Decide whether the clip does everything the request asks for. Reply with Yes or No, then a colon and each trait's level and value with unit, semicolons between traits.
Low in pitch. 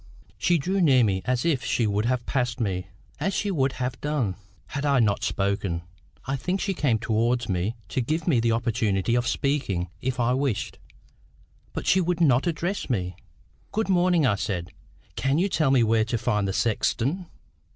Yes: low, 125 Hz